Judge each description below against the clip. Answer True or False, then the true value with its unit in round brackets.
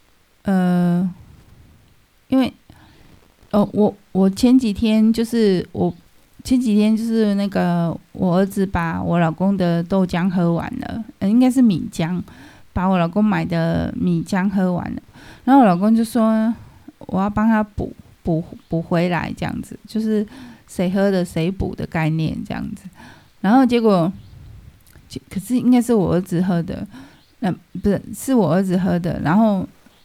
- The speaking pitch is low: False (195 Hz)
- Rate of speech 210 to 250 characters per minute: True (215 characters per minute)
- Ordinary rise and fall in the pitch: True (4.3 semitones)